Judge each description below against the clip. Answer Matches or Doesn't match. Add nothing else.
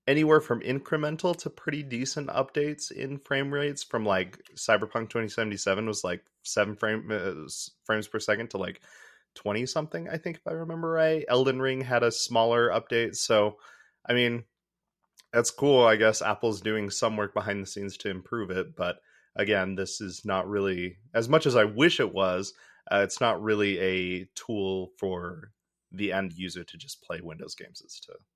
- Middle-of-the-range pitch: Doesn't match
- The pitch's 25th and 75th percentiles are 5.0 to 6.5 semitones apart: Matches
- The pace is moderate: Matches